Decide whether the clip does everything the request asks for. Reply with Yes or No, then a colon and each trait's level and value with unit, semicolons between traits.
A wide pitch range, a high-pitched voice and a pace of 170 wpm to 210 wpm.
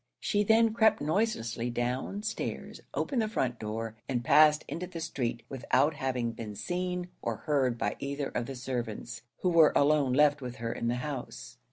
No: wide, 6.6 semitones; low, 135 Hz; average, 180 wpm